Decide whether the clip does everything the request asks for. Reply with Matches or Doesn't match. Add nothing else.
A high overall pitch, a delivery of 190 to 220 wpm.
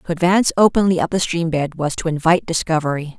Doesn't match